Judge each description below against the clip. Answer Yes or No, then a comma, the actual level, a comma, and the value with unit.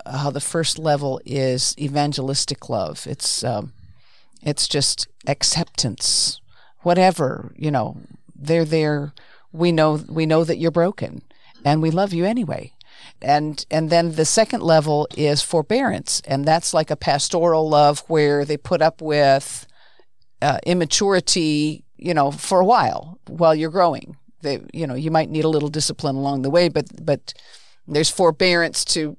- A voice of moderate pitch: Yes, medium, 155 Hz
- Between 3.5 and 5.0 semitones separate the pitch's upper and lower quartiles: No, average, 2.7 semitones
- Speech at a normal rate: Yes, average, 155 wpm